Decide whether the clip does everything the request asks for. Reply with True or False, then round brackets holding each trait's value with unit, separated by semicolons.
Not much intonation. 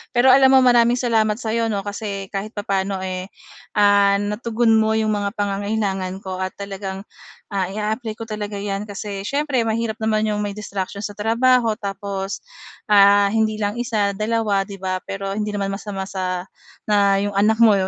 True (1.9 semitones)